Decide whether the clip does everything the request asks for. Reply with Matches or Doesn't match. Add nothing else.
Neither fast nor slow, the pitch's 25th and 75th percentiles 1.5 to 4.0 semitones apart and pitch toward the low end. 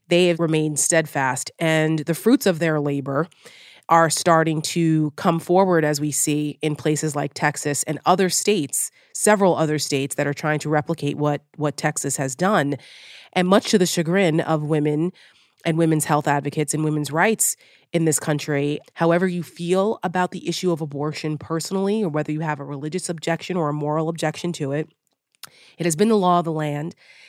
Doesn't match